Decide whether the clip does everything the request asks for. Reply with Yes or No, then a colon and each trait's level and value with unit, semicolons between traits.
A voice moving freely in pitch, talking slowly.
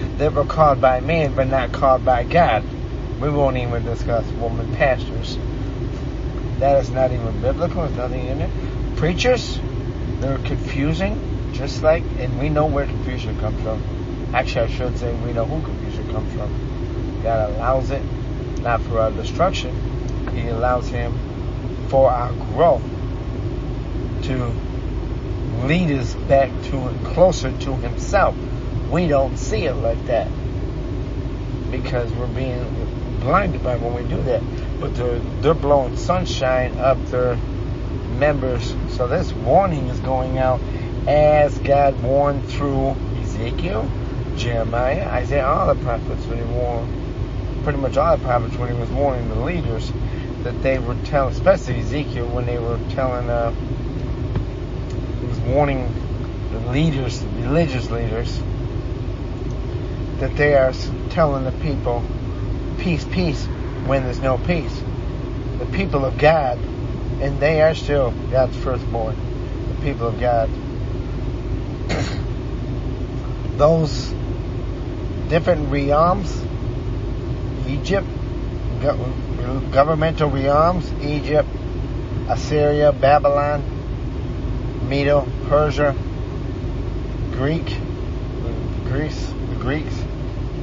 No: narrow, 2.5 semitones; slow, 120 wpm